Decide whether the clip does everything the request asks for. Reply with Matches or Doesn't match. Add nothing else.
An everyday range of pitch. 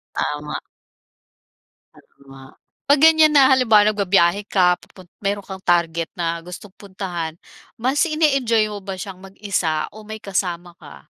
Matches